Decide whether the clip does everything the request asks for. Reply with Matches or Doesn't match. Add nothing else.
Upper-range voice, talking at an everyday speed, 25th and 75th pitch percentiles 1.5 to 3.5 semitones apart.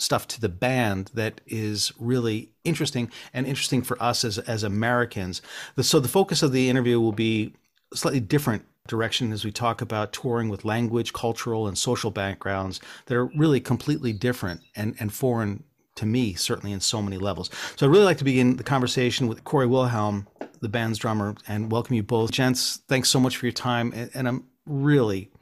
Doesn't match